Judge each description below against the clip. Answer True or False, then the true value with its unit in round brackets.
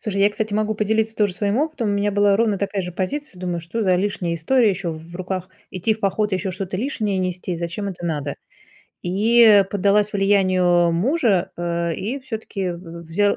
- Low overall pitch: False (195 Hz)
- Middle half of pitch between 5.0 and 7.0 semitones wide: False (3.1 semitones)